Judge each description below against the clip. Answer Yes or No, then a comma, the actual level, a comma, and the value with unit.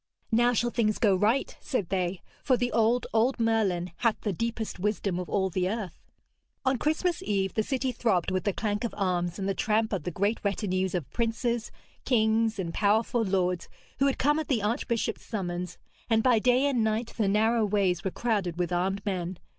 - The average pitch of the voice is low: No, high, 215 Hz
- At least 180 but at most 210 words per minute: Yes, average, 195 wpm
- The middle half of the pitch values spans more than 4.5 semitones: No, average, 3.8 semitones